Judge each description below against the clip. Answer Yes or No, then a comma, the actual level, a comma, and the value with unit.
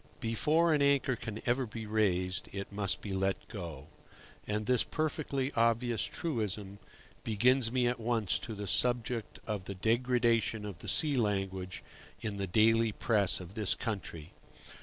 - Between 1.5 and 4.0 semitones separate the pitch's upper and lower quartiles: Yes, average, 3.6 semitones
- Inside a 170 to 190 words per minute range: No, average, 155 wpm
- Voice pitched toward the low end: Yes, low, 110 Hz